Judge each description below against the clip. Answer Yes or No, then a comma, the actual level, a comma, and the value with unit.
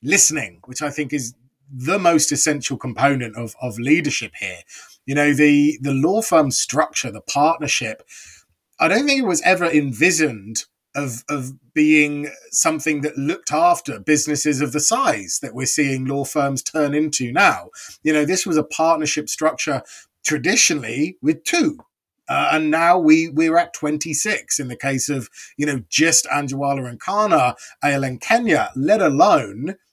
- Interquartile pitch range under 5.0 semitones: Yes, average, 2.7 semitones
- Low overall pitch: No, medium, 150 Hz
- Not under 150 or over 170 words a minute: Yes, average, 160 wpm